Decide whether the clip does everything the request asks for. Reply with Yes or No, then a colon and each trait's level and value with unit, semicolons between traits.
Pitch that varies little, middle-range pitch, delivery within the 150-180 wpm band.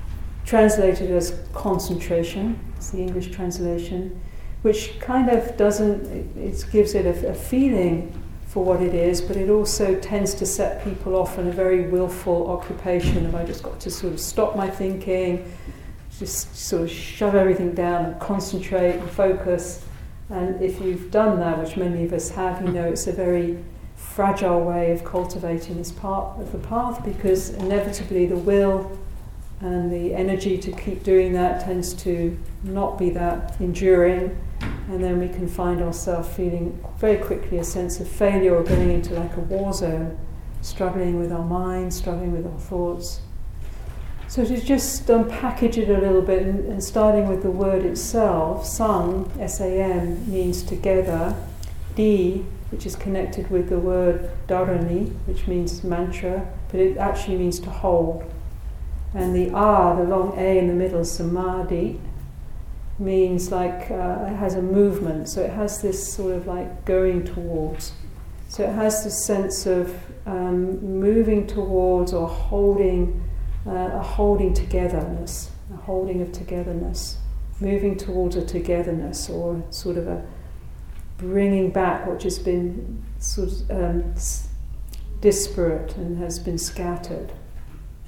Yes: narrow, 1.9 semitones; medium, 180 Hz; average, 155 wpm